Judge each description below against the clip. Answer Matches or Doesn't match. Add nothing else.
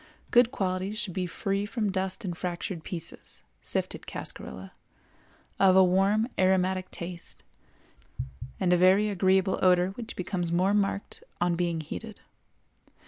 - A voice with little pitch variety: Matches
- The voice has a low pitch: Doesn't match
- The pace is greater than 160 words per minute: Doesn't match